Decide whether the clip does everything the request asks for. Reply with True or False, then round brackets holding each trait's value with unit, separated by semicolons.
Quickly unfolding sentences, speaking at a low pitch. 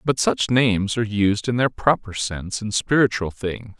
False (190 wpm; 105 Hz)